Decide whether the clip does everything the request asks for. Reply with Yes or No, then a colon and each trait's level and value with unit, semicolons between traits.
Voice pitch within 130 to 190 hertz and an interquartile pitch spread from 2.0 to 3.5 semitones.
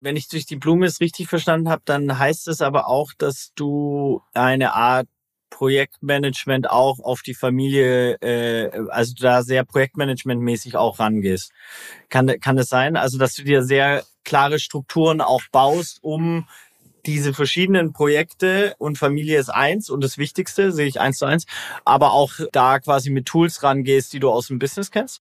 Yes: medium, 140 Hz; average, 3.1 semitones